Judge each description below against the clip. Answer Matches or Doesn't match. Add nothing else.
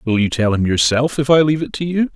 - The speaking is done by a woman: Doesn't match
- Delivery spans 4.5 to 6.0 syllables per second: Doesn't match